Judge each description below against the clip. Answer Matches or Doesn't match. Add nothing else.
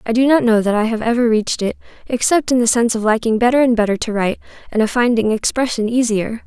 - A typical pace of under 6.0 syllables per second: Doesn't match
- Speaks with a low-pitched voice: Doesn't match